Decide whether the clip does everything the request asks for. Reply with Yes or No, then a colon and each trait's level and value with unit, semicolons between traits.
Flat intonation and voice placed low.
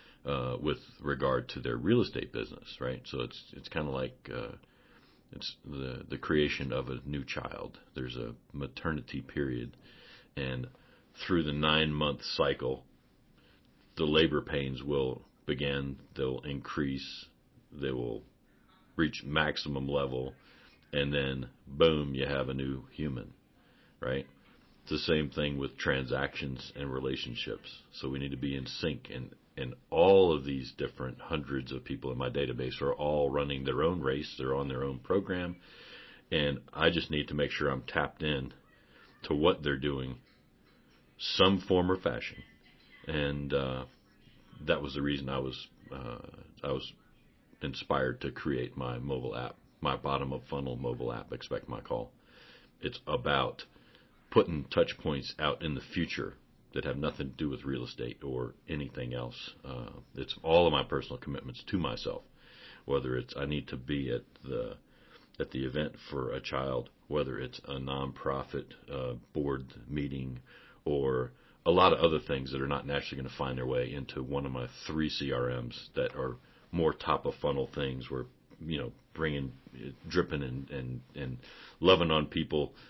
Yes: narrow, 2.0 semitones; very low, 70 Hz